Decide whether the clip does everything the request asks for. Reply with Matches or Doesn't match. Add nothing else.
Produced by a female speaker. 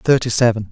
Doesn't match